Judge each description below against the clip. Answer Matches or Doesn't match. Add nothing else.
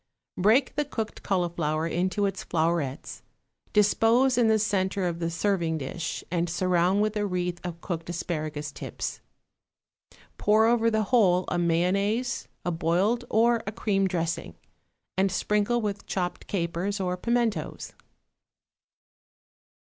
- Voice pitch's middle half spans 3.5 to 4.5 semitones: Matches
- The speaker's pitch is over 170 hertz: Matches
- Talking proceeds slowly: Matches